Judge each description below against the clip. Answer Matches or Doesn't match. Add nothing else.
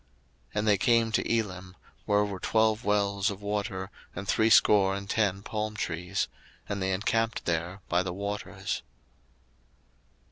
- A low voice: Matches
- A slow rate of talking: Doesn't match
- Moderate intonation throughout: Doesn't match